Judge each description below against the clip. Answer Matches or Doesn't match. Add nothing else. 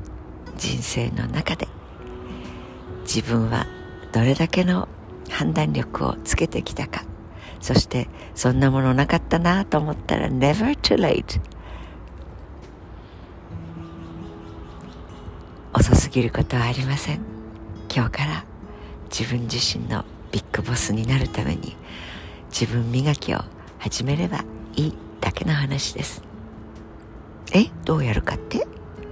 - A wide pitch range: Matches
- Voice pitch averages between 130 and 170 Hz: Doesn't match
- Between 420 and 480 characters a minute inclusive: Doesn't match